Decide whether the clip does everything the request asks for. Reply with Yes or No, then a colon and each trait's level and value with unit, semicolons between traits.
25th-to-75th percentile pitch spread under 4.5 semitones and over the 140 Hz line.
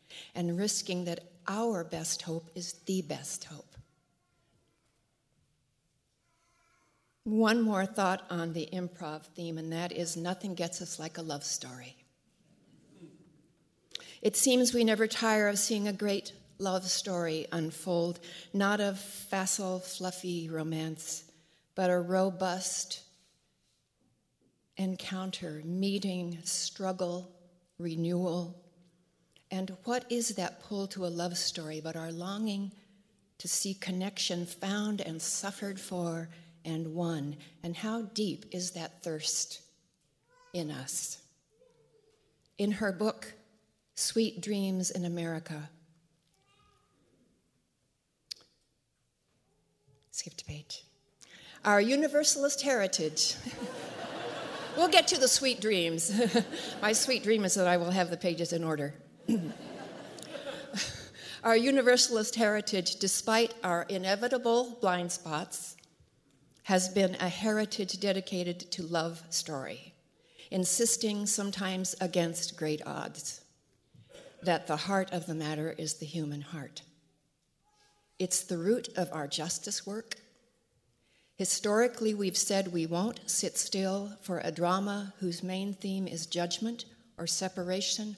Yes: average, 3.3 semitones; medium, 185 Hz